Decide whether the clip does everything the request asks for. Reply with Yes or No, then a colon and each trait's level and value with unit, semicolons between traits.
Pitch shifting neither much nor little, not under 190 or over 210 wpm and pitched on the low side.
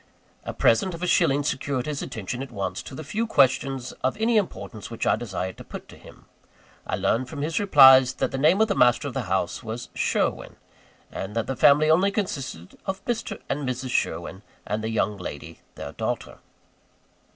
No: wide, 5.7 semitones; average, 195 wpm; low, 130 Hz